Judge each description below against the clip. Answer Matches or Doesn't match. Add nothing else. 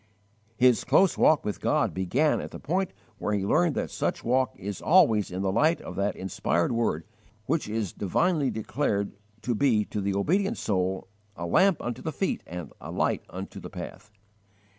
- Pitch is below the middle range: Matches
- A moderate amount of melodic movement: Doesn't match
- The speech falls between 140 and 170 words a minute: Doesn't match